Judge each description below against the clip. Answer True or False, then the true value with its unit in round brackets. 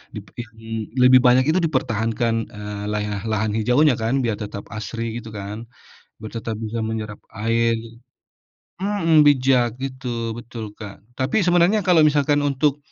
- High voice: False (115 Hz)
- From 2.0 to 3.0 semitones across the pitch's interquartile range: False (3.5 semitones)